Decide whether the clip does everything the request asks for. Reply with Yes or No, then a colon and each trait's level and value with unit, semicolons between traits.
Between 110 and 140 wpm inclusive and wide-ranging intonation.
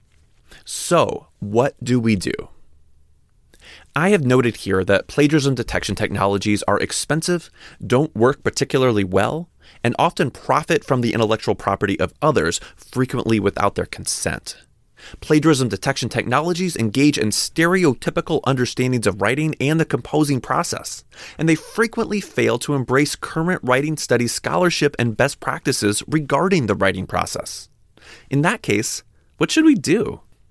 Yes: slow, 135 wpm; wide, 6.4 semitones